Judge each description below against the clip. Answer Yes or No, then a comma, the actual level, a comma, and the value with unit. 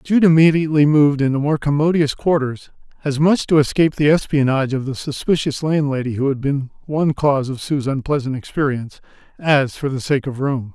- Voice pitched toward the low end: No, medium, 145 Hz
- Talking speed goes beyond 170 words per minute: Yes, average, 180 wpm